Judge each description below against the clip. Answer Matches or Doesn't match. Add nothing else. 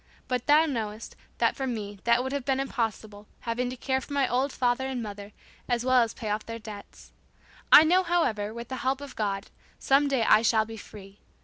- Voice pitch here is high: Matches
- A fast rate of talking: Matches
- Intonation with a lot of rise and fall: Doesn't match